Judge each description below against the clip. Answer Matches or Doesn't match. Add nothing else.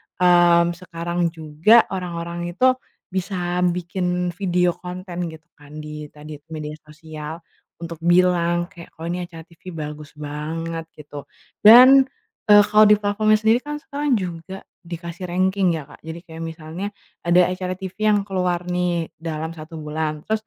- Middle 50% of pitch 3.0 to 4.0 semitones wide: Doesn't match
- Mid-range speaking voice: Matches